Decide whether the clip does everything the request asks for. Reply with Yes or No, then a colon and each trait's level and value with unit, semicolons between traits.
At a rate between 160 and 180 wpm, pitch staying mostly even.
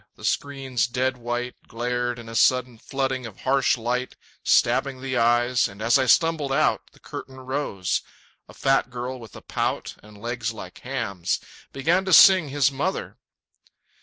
Yes: average, 165 wpm; narrow, 2.3 semitones